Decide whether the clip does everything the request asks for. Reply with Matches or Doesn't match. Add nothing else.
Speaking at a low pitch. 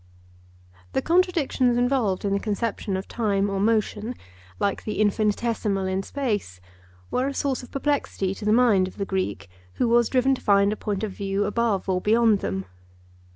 Doesn't match